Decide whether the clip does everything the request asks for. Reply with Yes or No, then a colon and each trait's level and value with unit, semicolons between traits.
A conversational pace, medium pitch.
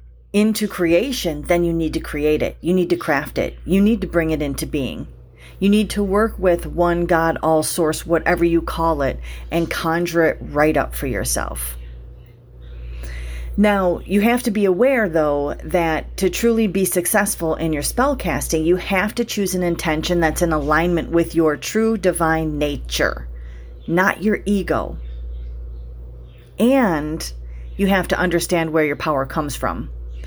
Yes: average, 165 wpm; medium, 165 Hz